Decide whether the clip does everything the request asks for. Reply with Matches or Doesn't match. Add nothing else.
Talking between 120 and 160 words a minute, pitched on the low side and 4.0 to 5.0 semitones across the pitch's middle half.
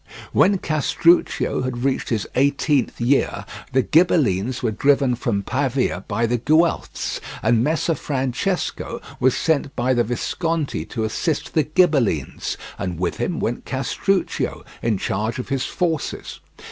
Matches